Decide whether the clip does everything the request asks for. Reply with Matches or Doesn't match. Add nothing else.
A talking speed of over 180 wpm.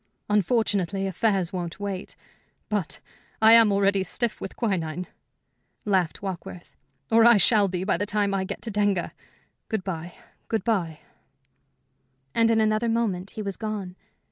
Doesn't match